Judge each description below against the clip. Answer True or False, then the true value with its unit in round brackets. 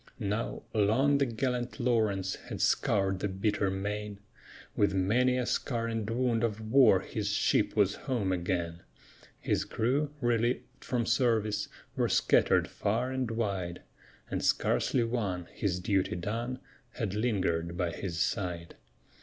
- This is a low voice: True (105 Hz)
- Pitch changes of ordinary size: True (3.9 semitones)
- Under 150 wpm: True (135 wpm)